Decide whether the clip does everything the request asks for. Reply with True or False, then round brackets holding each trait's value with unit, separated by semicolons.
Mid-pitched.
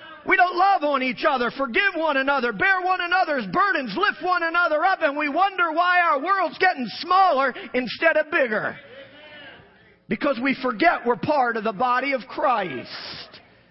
False (310 Hz)